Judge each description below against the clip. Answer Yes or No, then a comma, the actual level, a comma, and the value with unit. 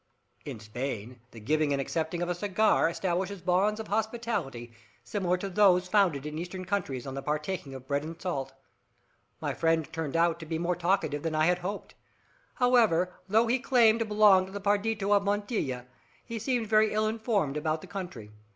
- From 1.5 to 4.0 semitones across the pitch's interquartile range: No, average, 5.3 semitones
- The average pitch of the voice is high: No, medium, 180 Hz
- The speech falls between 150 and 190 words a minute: Yes, average, 180 wpm